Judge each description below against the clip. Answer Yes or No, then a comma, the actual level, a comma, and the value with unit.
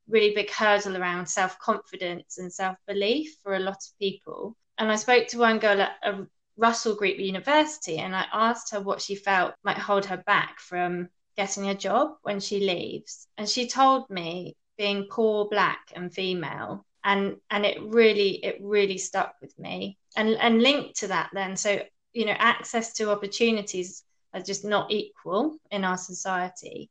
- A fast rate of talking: No, average, 175 wpm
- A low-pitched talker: No, high, 200 Hz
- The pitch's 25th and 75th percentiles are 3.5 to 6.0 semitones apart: No, average, 2.7 semitones